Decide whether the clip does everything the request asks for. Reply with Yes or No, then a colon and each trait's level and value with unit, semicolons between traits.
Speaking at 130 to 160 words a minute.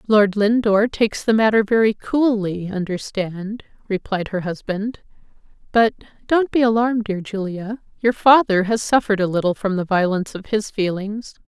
Yes: average, 140 wpm